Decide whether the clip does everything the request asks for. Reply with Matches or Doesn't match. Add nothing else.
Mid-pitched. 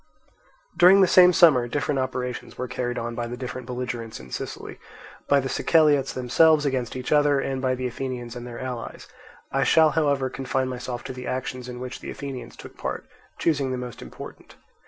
Doesn't match